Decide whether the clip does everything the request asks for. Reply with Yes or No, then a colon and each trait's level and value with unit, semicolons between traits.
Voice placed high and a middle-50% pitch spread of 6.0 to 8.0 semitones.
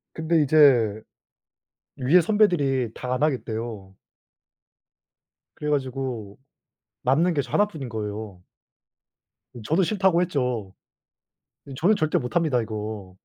No: low, 130 Hz; wide, 6.5 semitones